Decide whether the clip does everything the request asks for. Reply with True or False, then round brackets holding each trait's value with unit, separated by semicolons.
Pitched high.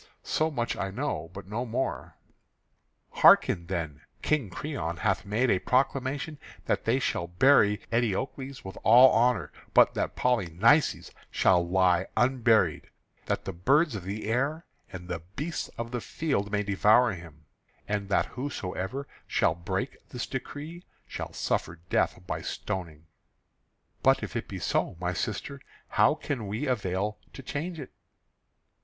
False (110 Hz)